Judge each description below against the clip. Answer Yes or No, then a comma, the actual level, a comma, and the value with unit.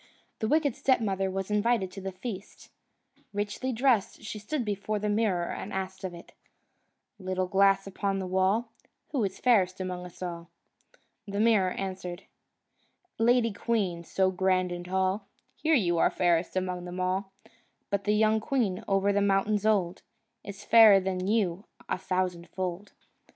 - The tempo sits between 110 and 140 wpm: No, average, 155 wpm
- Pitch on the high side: Yes, high, 195 Hz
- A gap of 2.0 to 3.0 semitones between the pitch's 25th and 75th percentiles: Yes, narrow, 2.5 semitones